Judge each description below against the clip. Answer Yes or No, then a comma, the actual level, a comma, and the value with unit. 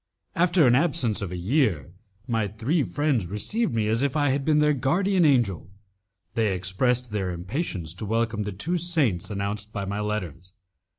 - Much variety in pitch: Yes, wide, 6.6 semitones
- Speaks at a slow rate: No, average, 175 wpm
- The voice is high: No, low, 115 Hz